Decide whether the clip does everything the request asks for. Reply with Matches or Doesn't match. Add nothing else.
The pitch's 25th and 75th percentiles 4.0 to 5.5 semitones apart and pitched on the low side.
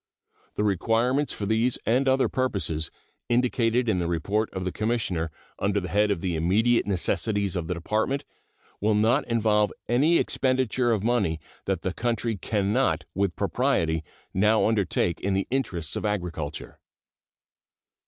Matches